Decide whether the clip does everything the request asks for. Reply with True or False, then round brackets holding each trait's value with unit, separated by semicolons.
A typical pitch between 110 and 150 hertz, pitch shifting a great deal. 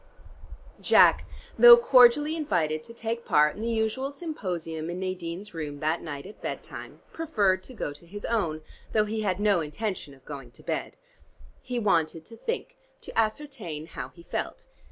False (200 Hz; 6.5 semitones)